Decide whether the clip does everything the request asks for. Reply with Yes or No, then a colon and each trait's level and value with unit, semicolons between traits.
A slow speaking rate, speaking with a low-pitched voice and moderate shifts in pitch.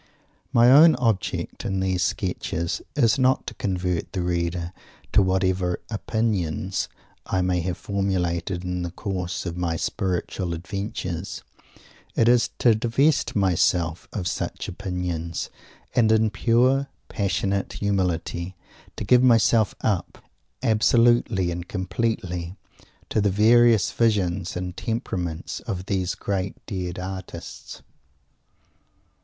Yes: slow, 115 wpm; very low, 95 Hz; average, 3.7 semitones